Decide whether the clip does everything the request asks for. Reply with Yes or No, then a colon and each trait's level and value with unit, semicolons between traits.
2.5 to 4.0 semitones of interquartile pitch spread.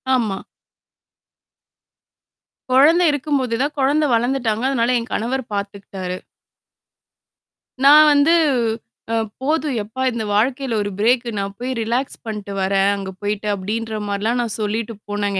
No: average, 4.5 semitones